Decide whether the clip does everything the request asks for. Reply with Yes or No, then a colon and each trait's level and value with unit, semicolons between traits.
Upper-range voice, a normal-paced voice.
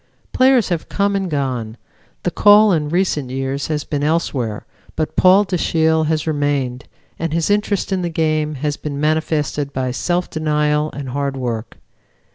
No: medium, 155 Hz; average, 160 wpm